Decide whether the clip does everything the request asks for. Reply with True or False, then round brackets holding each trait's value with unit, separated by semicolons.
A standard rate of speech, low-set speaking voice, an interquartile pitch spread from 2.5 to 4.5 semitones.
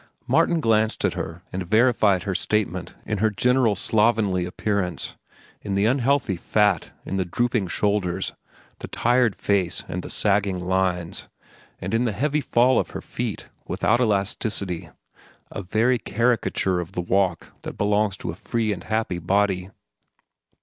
True (150 wpm; 100 Hz; 3.5 semitones)